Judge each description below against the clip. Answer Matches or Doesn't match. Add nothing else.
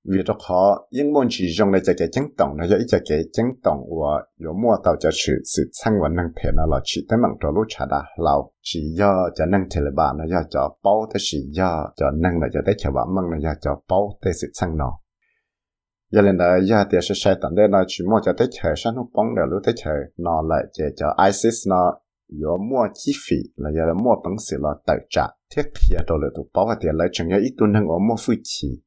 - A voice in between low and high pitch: Doesn't match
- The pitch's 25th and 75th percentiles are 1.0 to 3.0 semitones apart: Doesn't match